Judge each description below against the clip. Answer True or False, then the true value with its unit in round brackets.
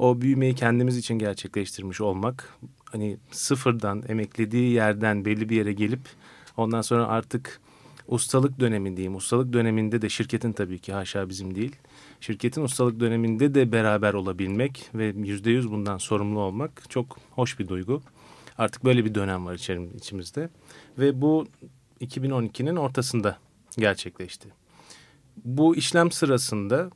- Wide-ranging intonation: False (3.8 semitones)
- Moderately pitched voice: False (115 Hz)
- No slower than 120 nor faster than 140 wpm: True (130 wpm)